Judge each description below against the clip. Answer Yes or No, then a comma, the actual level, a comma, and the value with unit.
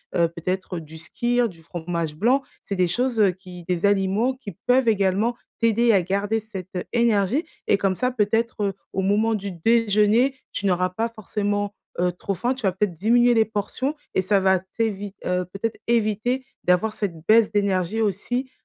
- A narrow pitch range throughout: No, average, 3.7 semitones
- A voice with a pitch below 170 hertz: No, high, 205 Hz